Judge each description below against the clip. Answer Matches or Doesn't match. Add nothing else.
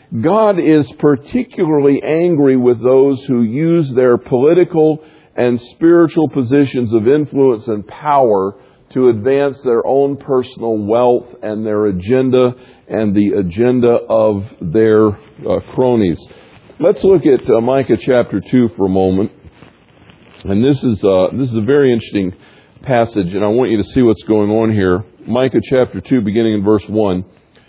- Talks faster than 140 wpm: Matches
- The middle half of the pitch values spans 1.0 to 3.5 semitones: Doesn't match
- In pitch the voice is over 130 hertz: Doesn't match